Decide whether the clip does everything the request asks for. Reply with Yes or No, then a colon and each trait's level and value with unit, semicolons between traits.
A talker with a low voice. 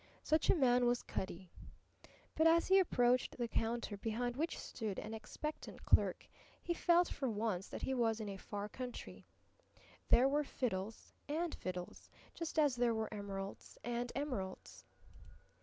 No: high, 240 Hz